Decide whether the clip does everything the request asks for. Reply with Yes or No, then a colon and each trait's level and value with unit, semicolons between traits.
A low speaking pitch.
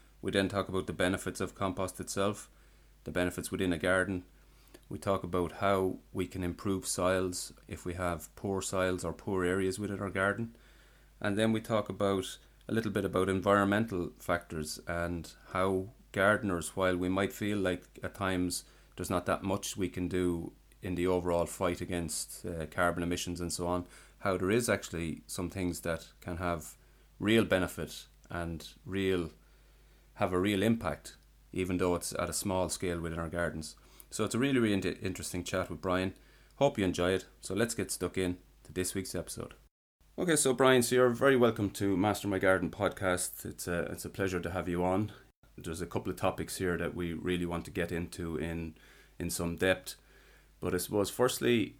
Yes: very low, 90 Hz